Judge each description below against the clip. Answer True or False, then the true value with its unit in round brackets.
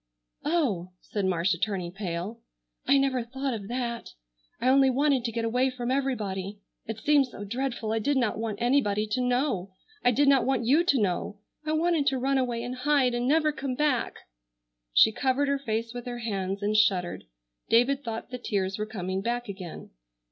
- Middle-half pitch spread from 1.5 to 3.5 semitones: False (4.5 semitones)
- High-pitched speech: True (240 Hz)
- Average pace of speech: True (190 wpm)